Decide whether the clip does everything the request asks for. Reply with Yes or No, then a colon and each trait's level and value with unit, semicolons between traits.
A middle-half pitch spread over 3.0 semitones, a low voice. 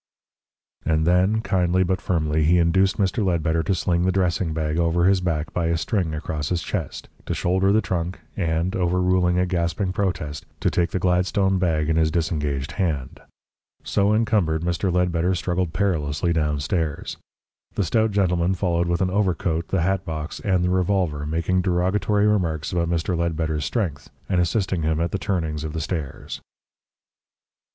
No: narrow, 2.6 semitones; very low, 85 Hz